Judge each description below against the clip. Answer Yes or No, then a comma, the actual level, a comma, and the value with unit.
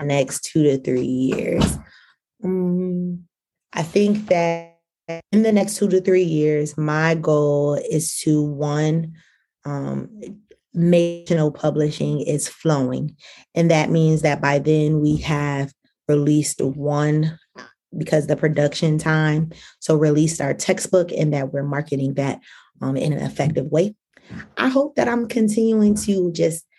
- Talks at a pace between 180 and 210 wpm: No, average, 145 wpm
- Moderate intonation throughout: Yes, average, 3.3 semitones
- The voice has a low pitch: No, medium, 155 Hz